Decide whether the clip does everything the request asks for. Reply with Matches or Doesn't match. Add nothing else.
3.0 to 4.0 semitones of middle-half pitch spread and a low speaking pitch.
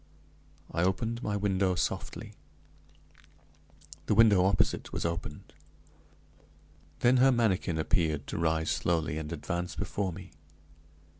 Matches